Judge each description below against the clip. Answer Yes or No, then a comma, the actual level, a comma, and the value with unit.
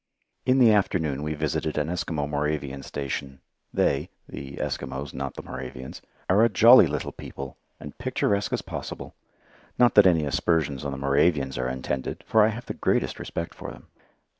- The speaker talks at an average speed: Yes, average, 170 wpm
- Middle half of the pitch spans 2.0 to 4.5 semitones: No, average, 5.1 semitones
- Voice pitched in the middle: No, very low, 75 Hz